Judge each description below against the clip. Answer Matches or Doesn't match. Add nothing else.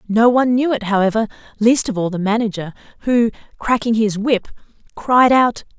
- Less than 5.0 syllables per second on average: Doesn't match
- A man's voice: Doesn't match